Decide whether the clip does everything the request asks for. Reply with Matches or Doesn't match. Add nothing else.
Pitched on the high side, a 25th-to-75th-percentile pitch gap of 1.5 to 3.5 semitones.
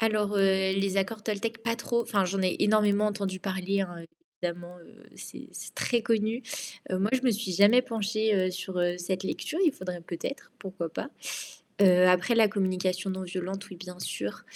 Matches